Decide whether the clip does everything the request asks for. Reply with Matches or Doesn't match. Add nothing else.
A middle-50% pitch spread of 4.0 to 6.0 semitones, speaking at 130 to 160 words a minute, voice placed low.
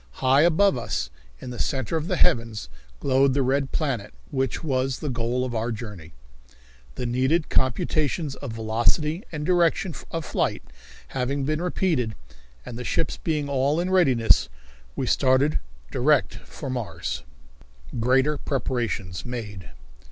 Matches